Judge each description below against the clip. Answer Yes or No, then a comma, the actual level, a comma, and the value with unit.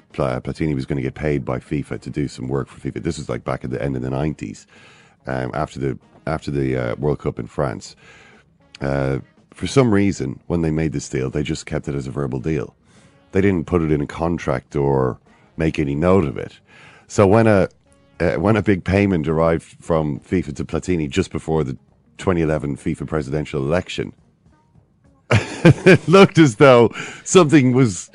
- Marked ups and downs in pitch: Yes, wide, 5.8 semitones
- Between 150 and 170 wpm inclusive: No, average, 195 wpm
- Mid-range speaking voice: No, very low, 80 Hz